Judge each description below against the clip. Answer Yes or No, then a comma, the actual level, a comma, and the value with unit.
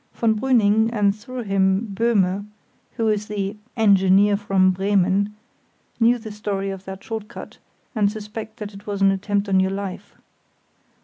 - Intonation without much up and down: Yes, narrow, 1.9 semitones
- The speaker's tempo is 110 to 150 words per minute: No, average, 160 wpm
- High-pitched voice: Yes, high, 205 Hz